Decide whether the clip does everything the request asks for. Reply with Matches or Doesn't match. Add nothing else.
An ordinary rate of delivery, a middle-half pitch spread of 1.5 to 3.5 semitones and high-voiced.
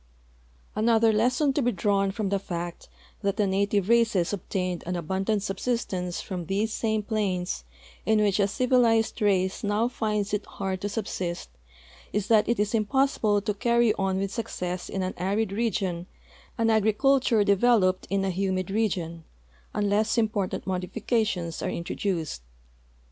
Matches